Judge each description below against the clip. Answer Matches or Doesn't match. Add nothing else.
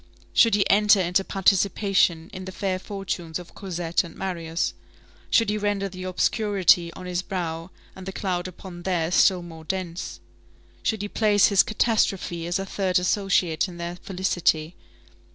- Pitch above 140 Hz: Matches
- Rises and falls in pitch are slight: Matches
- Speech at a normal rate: Matches